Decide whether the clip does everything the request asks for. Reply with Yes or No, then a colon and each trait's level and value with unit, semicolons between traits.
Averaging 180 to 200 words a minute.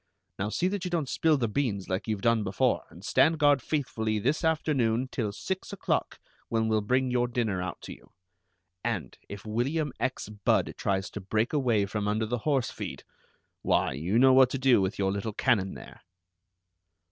Yes: average, 190 wpm